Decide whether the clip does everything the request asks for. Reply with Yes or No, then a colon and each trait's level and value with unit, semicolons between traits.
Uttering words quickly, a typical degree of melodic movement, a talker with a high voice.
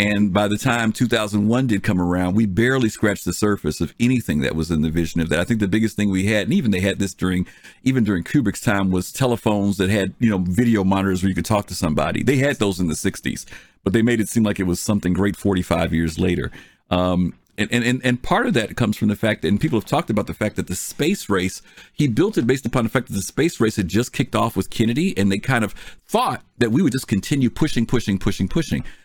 No: fast, 260 wpm; average, 3.9 semitones; low, 105 Hz